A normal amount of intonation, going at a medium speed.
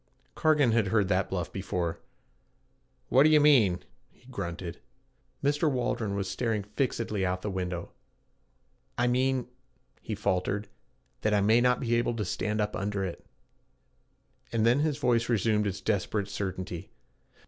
Yes: average, 4.3 semitones; average, 150 wpm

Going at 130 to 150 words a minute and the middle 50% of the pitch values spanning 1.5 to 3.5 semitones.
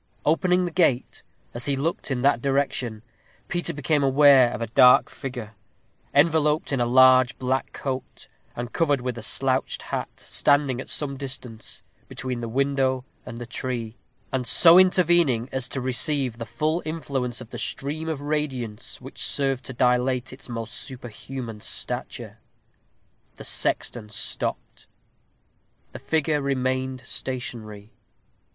Yes: average, 140 wpm; average, 2.8 semitones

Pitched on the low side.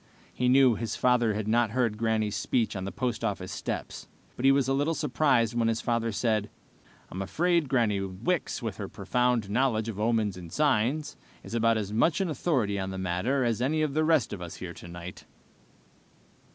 Yes: low, 115 Hz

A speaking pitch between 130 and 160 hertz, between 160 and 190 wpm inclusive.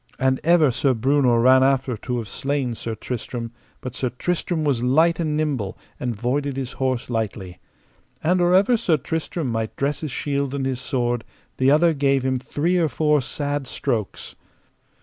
Yes: low, 135 Hz; average, 175 wpm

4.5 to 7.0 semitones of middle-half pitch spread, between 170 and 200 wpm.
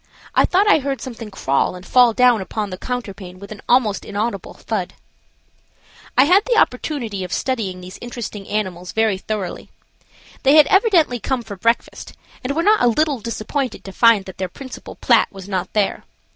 Yes: average, 5.0 semitones; average, 180 wpm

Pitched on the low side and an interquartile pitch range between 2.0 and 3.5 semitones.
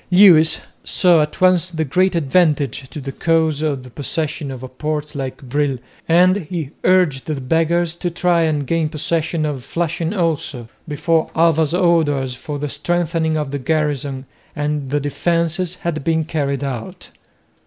No: medium, 155 Hz; average, 3.0 semitones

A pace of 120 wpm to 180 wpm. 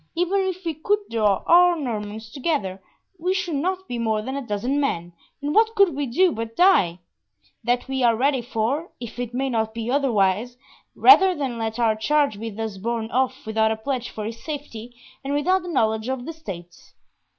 No: average, 195 wpm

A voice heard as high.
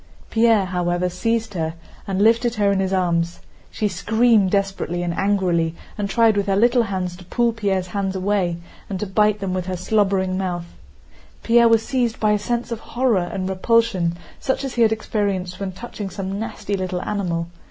Yes: high, 195 Hz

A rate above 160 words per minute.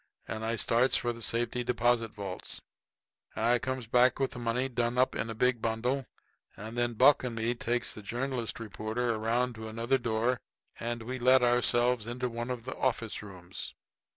Yes: average, 180 wpm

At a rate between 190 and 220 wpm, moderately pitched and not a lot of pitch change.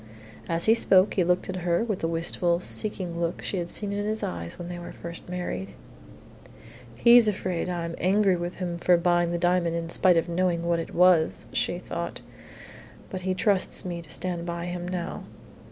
Yes: average, 195 wpm; medium, 175 Hz; narrow, 1.5 semitones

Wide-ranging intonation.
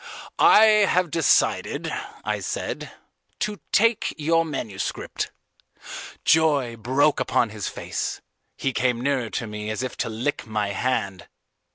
Yes: wide, 6.6 semitones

